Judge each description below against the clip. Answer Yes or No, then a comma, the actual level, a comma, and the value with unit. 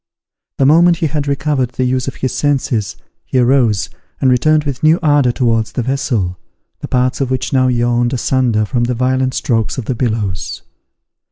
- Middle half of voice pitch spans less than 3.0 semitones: Yes, narrow, 2.4 semitones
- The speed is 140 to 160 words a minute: No, average, 180 wpm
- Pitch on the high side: No, low, 130 Hz